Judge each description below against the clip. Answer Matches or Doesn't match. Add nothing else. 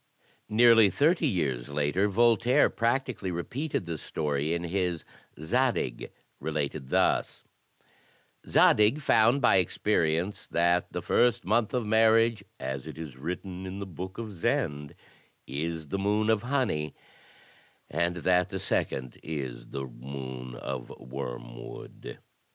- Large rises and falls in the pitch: Matches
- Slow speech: Matches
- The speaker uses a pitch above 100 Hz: Doesn't match